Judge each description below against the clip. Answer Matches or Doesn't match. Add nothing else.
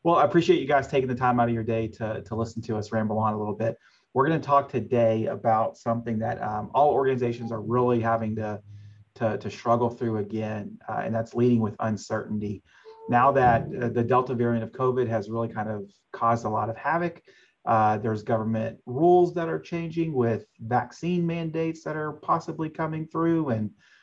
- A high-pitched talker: Doesn't match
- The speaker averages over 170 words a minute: Matches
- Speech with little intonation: Doesn't match